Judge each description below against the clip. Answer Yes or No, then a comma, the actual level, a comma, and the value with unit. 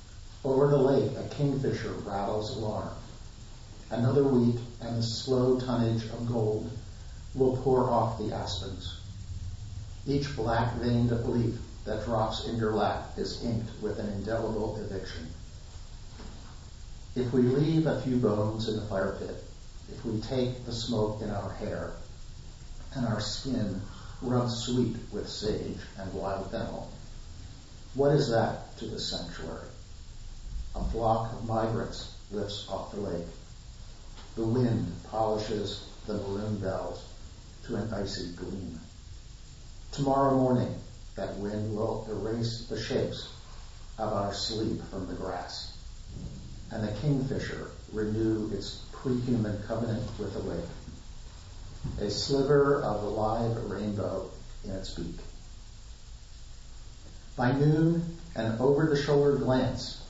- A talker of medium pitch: No, low, 110 Hz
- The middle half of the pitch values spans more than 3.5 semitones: No, average, 3.1 semitones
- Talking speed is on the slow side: Yes, slow, 125 wpm